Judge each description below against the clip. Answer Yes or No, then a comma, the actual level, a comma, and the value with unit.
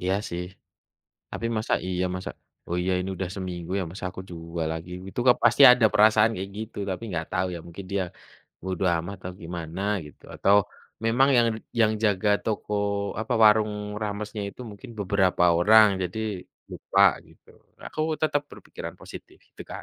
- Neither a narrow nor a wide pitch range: Yes, average, 3.4 semitones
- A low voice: Yes, very low, 95 Hz